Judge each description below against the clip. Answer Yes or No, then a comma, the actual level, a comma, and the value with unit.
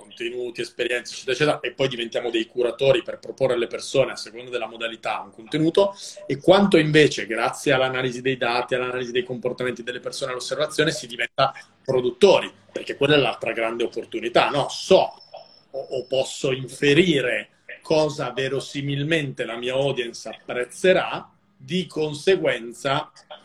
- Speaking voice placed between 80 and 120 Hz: No, low, 135 Hz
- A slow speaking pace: No, average, 140 wpm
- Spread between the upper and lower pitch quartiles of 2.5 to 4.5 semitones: No, average, 5.3 semitones